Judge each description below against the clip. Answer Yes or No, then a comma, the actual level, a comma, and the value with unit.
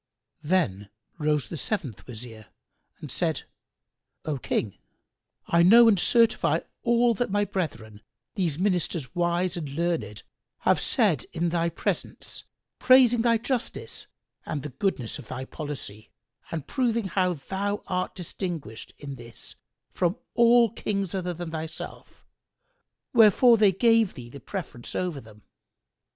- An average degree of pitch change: No, wide, 6.6 semitones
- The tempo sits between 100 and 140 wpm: Yes, slow, 135 wpm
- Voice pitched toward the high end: No, medium, 175 Hz